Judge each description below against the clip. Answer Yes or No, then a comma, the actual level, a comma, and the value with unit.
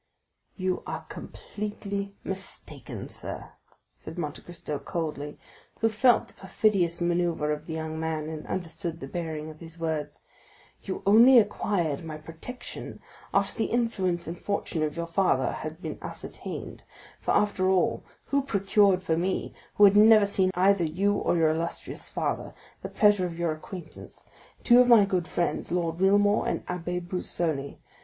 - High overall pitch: No, medium, 180 Hz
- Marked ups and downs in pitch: No, average, 3.8 semitones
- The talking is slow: No, average, 155 wpm